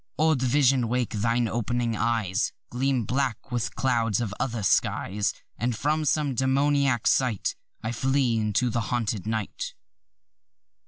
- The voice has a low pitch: Yes, low, 120 Hz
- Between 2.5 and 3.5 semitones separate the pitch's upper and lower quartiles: Yes, average, 3.0 semitones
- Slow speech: Yes, slow, 130 wpm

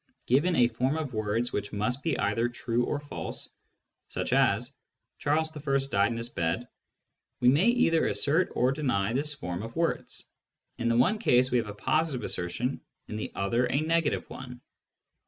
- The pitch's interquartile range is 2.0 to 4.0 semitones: No, average, 4.8 semitones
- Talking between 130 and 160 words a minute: No, average, 180 wpm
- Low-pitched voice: Yes, low, 125 Hz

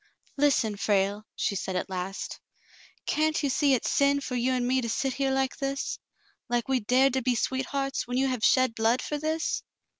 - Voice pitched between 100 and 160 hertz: No, very high, 260 Hz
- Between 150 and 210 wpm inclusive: Yes, fast, 205 wpm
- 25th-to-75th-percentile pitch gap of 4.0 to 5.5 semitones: No, average, 3.1 semitones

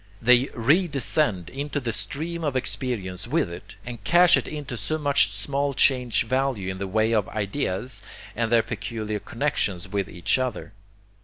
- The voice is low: Yes, low, 120 Hz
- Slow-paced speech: No, average, 160 wpm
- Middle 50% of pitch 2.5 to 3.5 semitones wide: No, wide, 5.4 semitones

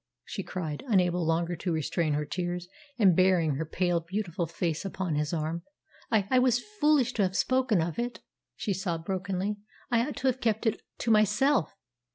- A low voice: No, medium, 185 Hz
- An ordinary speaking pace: Yes, average, 185 wpm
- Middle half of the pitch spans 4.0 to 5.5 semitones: Yes, average, 4.9 semitones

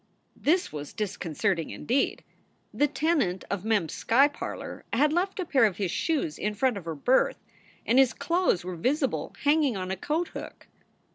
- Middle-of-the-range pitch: No, high, 245 Hz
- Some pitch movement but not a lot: No, wide, 7.8 semitones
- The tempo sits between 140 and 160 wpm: No, average, 185 wpm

